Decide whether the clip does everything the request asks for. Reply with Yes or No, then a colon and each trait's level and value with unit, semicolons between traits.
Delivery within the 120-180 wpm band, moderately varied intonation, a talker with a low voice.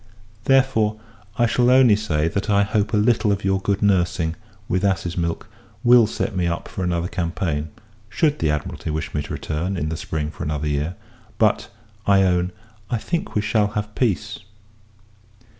Yes: average, 175 wpm; average, 4.3 semitones; very low, 95 Hz